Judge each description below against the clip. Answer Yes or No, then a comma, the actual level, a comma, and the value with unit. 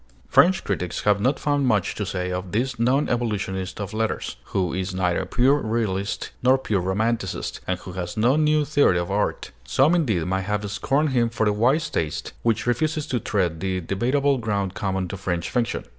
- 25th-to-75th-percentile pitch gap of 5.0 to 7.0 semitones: Yes, wide, 5.4 semitones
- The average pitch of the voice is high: No, low, 105 Hz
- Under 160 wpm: No, average, 190 wpm